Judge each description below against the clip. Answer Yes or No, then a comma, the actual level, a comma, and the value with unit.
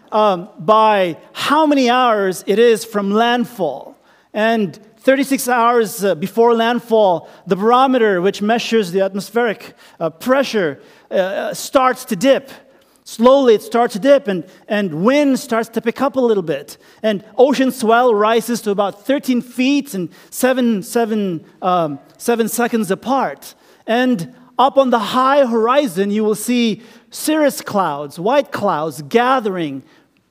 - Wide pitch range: No, average, 3.8 semitones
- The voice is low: No, high, 230 Hz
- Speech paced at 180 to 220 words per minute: No, average, 140 wpm